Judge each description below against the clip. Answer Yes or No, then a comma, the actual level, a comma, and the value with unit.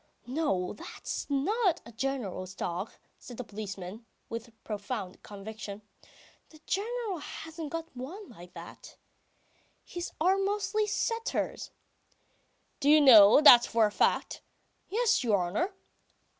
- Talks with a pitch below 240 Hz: No, very high, 255 Hz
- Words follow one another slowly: Yes, slow, 120 wpm